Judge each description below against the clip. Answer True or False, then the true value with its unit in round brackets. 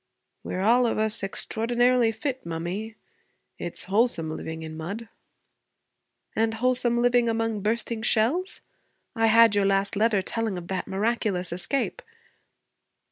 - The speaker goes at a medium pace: False (130 wpm)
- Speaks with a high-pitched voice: True (220 Hz)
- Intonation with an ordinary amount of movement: True (3.4 semitones)